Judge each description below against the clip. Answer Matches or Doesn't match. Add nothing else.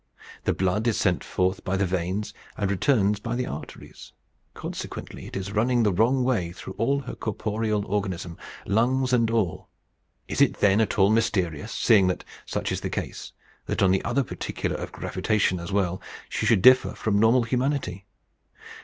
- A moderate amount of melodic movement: Matches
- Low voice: Matches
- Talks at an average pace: Matches